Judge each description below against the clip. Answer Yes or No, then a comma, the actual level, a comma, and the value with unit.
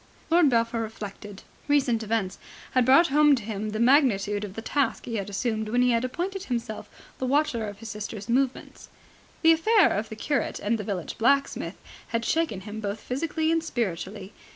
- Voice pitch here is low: No, high, 230 Hz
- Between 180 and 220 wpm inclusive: Yes, average, 185 wpm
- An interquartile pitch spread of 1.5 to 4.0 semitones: No, average, 4.8 semitones